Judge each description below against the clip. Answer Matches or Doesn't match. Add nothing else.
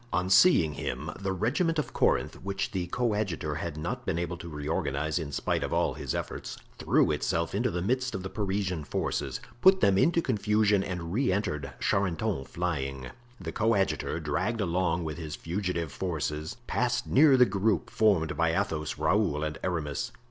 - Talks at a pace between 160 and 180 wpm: Matches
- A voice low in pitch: Matches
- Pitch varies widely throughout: Doesn't match